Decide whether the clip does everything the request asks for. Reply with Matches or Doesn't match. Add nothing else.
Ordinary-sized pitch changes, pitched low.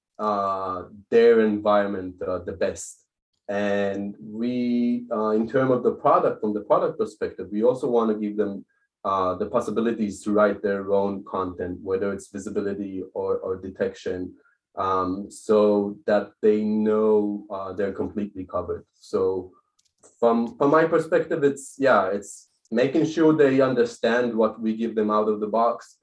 Matches